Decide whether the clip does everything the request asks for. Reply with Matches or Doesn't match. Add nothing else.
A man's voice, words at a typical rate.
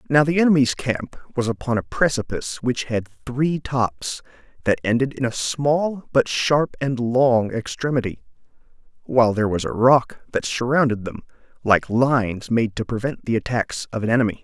Matches